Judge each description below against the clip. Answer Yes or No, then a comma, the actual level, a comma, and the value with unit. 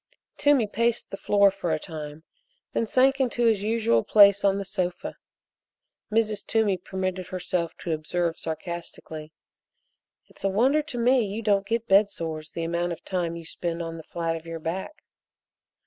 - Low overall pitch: No, high, 190 Hz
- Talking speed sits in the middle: Yes, average, 170 wpm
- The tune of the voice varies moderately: Yes, average, 4.5 semitones